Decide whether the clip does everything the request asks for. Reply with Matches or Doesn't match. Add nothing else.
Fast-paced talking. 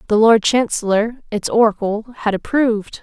Doesn't match